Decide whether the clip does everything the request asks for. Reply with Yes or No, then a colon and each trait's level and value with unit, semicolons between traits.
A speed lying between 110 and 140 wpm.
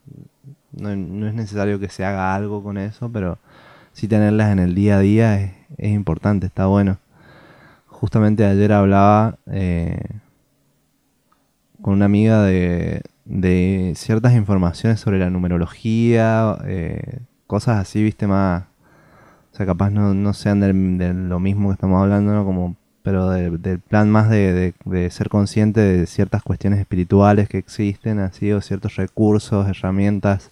No: average, 155 wpm